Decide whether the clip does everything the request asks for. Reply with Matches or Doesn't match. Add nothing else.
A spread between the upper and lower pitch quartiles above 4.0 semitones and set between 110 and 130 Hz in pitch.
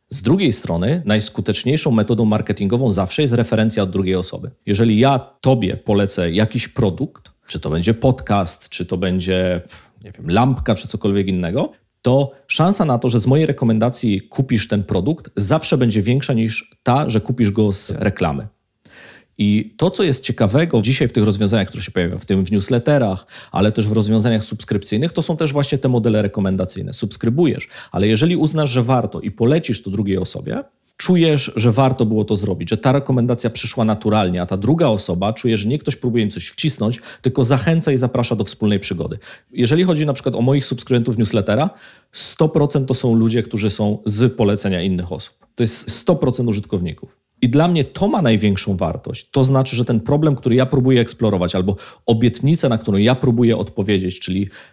Matches